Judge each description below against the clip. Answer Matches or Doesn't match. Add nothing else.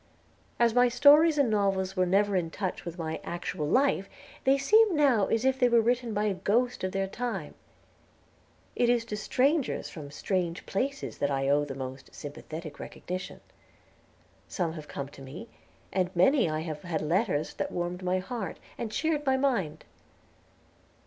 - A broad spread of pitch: Matches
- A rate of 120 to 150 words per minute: Doesn't match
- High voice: Matches